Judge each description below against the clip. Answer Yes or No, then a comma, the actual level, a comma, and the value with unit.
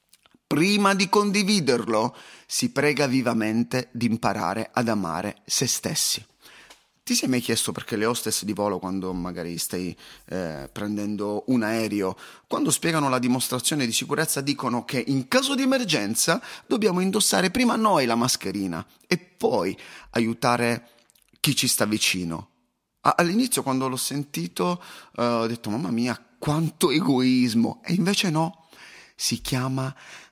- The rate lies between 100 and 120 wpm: No, average, 140 wpm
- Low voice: Yes, low, 120 Hz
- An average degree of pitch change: No, wide, 5.7 semitones